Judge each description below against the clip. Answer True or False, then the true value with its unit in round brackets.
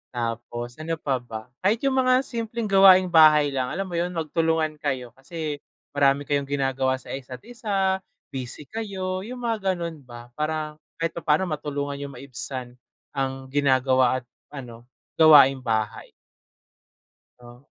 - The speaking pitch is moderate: True (145 Hz)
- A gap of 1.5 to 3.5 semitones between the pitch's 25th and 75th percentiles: False (5.2 semitones)